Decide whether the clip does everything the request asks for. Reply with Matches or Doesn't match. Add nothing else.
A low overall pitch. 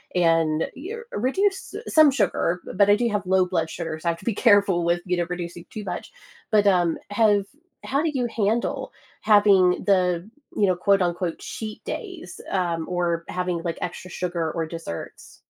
Doesn't match